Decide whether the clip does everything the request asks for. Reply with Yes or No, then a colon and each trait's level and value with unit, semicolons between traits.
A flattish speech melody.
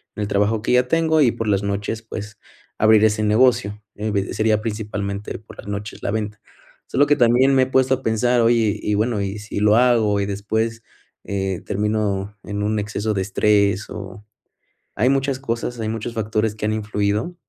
Yes: narrow, 2.2 semitones